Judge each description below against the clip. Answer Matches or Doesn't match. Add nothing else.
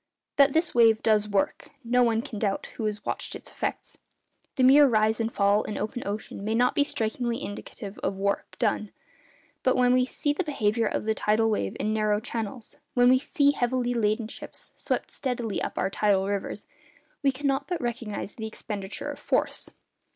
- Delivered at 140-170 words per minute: Doesn't match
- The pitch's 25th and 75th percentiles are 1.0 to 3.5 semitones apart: Matches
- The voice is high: Matches